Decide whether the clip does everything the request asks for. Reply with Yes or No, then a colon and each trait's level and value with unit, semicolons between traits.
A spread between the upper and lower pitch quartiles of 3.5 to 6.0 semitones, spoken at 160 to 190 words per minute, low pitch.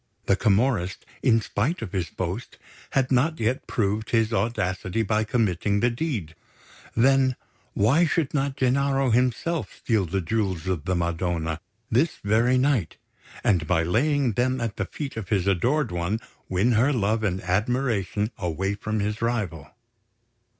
No: average, 5.2 semitones; average, 150 wpm; low, 110 Hz